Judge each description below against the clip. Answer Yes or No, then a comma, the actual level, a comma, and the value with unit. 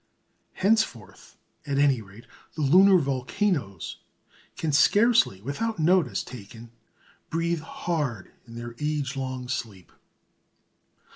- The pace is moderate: No, slow, 100 wpm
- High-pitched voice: No, medium, 140 Hz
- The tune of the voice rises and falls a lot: Yes, wide, 6.3 semitones